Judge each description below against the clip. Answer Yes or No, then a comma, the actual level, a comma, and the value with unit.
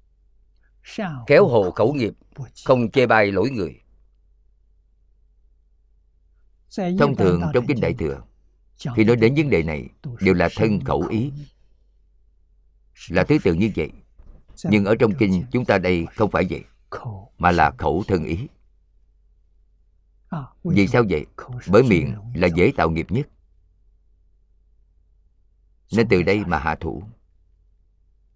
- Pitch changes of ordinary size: Yes, average, 3.9 semitones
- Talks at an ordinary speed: No, slow, 130 wpm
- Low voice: Yes, very low, 85 Hz